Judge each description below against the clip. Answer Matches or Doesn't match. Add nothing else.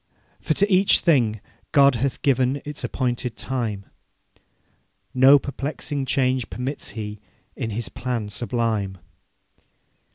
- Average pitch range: Matches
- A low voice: Matches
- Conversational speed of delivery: Doesn't match